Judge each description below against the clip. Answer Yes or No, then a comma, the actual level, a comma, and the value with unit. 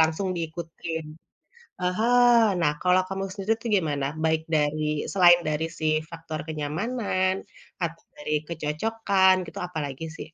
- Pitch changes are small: No, average, 3.4 semitones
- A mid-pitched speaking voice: Yes, medium, 165 Hz